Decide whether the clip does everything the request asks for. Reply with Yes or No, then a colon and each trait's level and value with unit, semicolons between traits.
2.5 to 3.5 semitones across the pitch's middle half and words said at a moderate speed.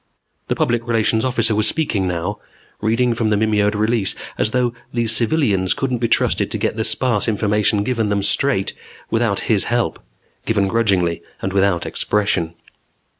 Yes: average, 2.8 semitones; average, 160 wpm